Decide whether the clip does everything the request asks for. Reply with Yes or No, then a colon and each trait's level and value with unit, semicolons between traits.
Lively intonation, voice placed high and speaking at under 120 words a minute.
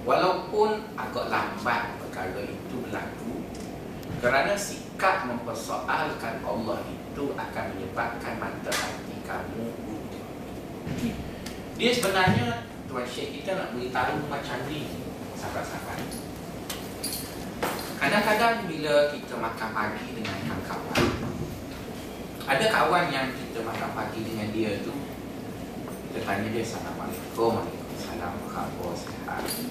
No: wide, 5.8 semitones; low, 115 Hz; average, 105 wpm